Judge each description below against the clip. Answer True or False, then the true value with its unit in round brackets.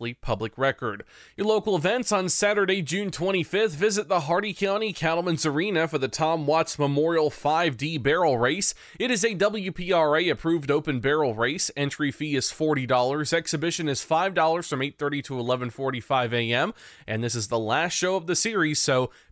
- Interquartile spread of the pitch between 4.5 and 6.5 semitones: True (5.1 semitones)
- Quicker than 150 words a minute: True (165 wpm)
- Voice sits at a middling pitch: True (160 Hz)